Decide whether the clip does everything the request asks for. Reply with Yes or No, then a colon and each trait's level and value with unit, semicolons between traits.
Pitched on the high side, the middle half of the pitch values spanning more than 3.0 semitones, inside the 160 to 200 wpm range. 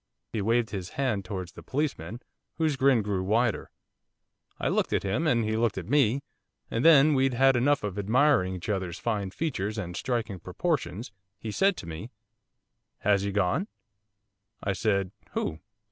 No: low, 110 Hz; wide, 5.5 semitones; average, 170 wpm